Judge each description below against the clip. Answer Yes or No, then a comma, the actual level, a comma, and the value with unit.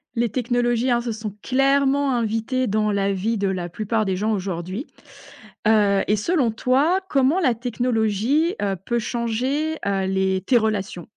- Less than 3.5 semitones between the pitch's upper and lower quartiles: No, average, 4.3 semitones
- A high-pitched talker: Yes, high, 225 Hz